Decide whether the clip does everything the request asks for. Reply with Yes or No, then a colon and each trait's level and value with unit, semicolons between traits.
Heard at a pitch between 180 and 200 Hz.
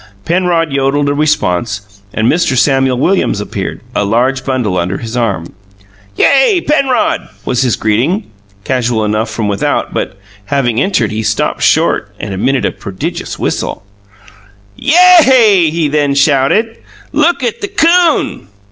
No: low, 135 Hz